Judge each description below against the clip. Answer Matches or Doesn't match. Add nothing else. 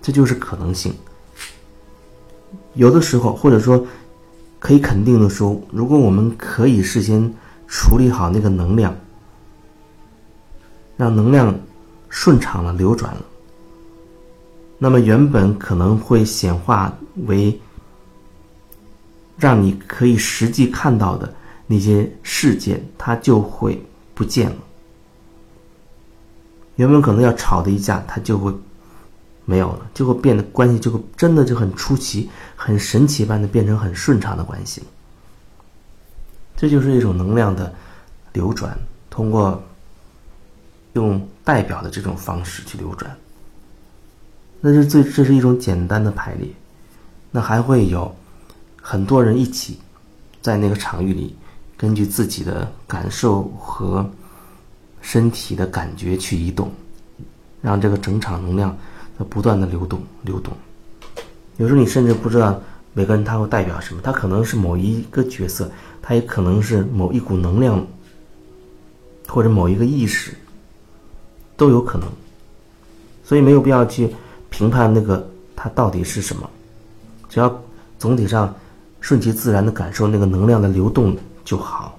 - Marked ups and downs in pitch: Doesn't match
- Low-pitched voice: Matches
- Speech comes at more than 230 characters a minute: Doesn't match